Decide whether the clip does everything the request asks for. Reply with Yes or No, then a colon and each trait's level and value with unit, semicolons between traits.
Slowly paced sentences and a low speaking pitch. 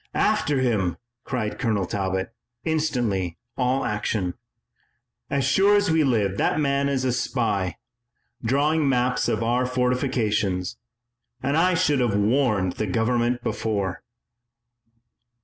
Yes: slow, 120 wpm; low, 125 Hz